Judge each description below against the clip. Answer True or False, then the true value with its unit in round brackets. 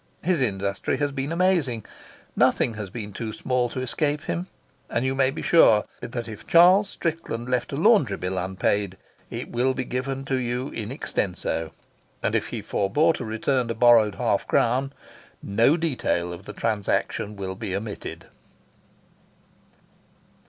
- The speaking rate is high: False (145 wpm)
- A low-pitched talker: True (120 Hz)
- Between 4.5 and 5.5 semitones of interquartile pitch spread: True (4.9 semitones)